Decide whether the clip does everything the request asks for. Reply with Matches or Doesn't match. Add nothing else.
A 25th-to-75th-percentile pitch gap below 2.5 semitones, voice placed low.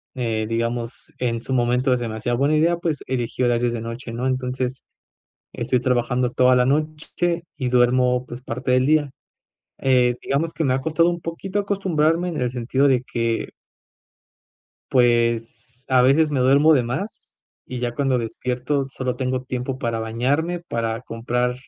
Doesn't match